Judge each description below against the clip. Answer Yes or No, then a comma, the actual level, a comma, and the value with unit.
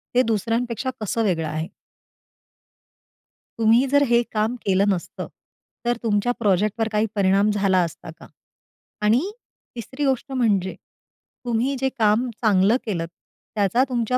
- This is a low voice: No, high, 220 Hz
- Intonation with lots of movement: No, average, 3.5 semitones